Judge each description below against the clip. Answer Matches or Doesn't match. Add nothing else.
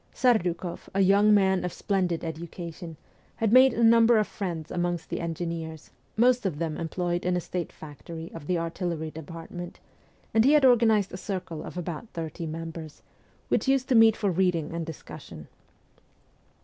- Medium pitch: Matches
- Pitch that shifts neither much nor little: Matches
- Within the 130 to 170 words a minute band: Matches